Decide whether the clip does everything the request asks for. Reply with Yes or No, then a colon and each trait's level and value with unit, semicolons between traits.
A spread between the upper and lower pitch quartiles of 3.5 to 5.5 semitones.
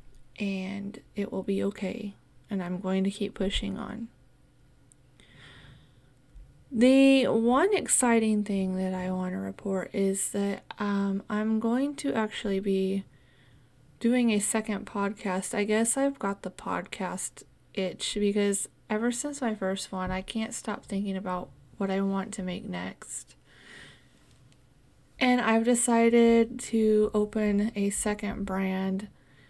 No: average, 2.9 semitones